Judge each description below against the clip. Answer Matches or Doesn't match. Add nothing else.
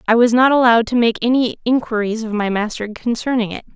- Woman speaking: Matches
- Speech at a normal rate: Doesn't match